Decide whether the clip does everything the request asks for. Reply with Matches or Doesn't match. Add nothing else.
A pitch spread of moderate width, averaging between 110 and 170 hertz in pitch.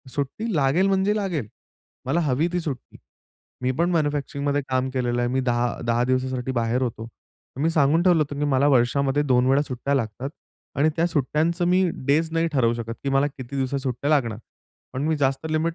Matches